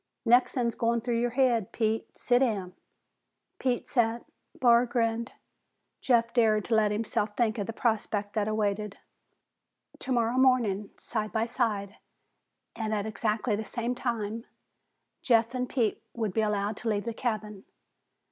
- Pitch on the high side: Yes, high, 225 Hz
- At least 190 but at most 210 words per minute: No, average, 140 wpm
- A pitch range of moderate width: No, narrow, 2.1 semitones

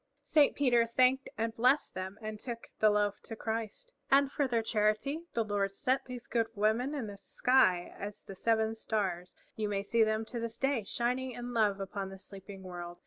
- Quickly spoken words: No, average, 195 wpm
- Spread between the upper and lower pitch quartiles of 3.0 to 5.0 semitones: Yes, average, 3.7 semitones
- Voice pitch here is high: Yes, high, 225 Hz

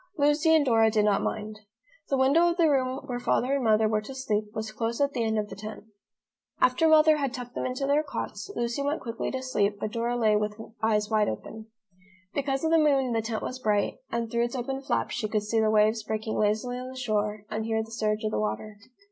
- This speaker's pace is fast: Yes, fast, 240 wpm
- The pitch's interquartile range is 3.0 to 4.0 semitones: Yes, average, 3.7 semitones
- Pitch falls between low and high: No, high, 230 Hz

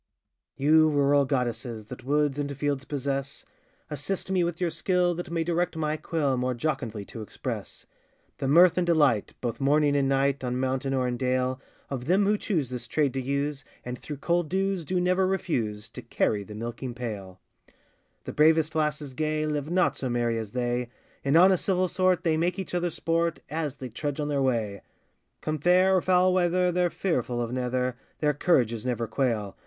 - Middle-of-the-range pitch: Yes, medium, 145 Hz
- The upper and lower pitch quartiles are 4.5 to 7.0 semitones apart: Yes, average, 5.2 semitones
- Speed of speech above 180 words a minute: Yes, average, 190 wpm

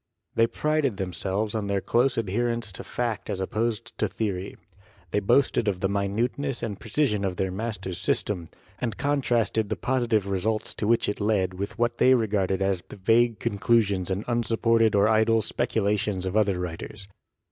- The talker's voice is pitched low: Yes, low, 105 Hz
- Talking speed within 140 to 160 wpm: No, average, 170 wpm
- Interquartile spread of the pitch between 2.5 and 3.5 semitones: Yes, average, 3.2 semitones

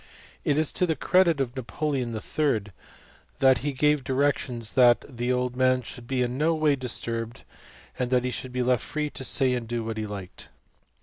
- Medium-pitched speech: No, low, 125 Hz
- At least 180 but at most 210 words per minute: Yes, average, 185 wpm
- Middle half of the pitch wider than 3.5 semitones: No, average, 3.0 semitones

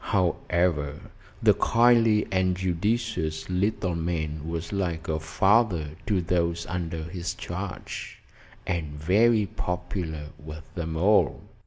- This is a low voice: Yes, very low, 90 Hz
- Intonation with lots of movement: No, average, 3.4 semitones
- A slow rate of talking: Yes, slow, 115 wpm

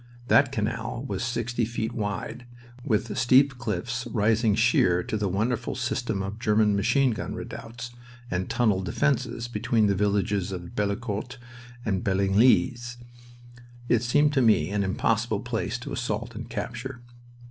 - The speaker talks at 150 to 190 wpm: No, average, 140 wpm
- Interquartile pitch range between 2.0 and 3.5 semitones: Yes, average, 3.0 semitones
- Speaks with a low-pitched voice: Yes, low, 115 Hz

